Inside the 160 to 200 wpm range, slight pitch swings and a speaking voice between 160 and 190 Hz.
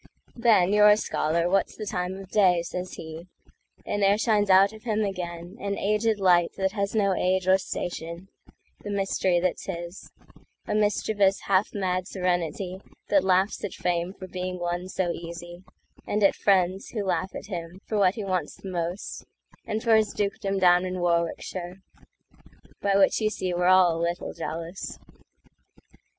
No: average, 150 wpm; narrow, 2.3 semitones; medium, 185 Hz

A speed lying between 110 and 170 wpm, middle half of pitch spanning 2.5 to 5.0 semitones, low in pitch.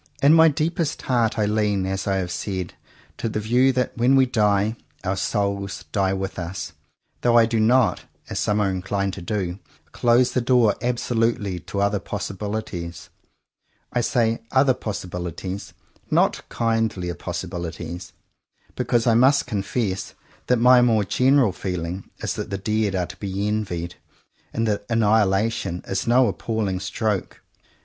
Yes: average, 150 wpm; average, 3.7 semitones; low, 105 Hz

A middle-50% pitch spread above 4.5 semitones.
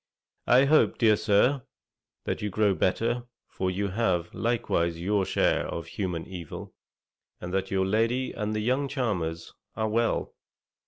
No: average, 4.1 semitones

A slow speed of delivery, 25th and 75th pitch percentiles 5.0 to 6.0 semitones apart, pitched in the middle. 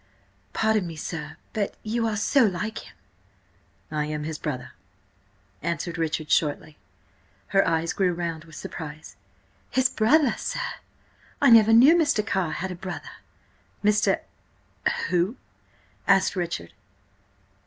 Yes: slow, 120 wpm; wide, 5.4 semitones; medium, 180 Hz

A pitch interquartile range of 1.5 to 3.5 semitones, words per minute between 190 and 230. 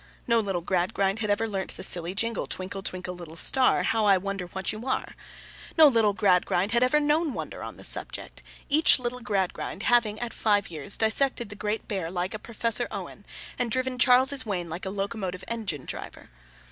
No: average, 4.2 semitones; average, 195 wpm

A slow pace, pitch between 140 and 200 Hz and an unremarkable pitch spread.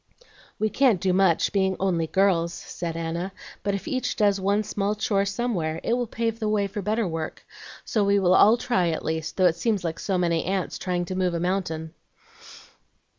No: average, 200 wpm; high, 190 Hz; average, 3.4 semitones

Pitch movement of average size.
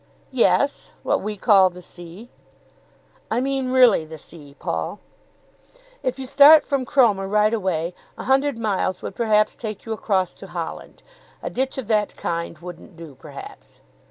No: wide, 6.3 semitones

